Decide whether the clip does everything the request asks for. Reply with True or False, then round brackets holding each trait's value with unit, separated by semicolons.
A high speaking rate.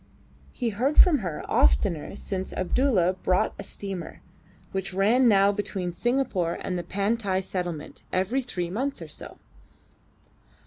False (135 wpm)